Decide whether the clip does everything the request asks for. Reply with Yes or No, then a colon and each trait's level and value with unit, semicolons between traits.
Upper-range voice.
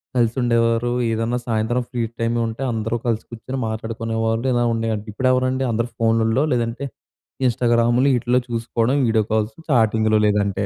No: low, 115 Hz